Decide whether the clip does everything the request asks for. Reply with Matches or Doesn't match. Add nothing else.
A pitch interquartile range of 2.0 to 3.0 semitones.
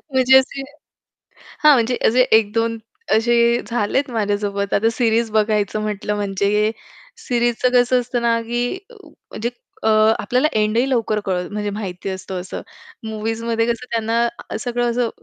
Matches